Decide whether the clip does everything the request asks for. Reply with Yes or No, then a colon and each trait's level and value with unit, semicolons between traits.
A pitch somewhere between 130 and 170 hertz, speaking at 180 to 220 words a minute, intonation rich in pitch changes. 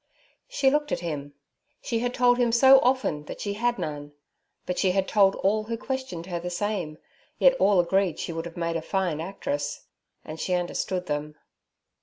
No: high, 190 Hz; average, 190 wpm; wide, 6.3 semitones